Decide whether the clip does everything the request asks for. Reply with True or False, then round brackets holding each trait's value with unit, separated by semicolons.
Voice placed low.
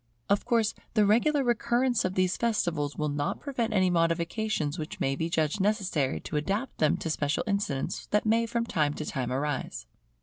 False (185 Hz)